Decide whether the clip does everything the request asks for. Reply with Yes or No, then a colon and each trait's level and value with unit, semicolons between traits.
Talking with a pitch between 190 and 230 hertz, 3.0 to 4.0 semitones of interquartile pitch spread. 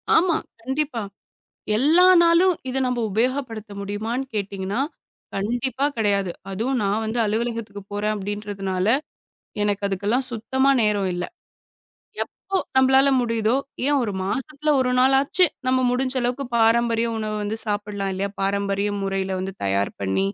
No: high, 225 Hz; average, 4.5 semitones